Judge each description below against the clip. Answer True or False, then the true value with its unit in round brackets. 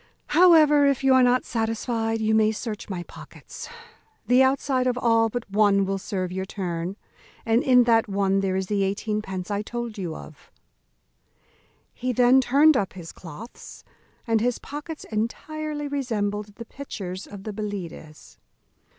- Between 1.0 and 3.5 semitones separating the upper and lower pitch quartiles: False (4.4 semitones)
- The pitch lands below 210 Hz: False (220 Hz)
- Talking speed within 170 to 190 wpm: False (160 wpm)